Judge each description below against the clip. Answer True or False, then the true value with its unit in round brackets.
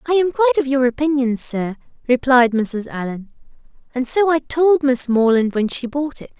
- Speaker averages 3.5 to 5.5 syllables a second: True (5.0 syllables/s)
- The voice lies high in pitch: True (265 Hz)